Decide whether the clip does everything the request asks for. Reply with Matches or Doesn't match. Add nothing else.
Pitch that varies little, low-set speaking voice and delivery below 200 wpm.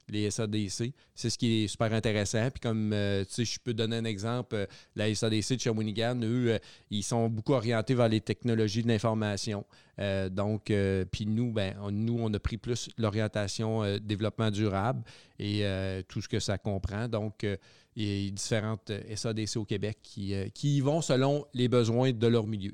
Doesn't match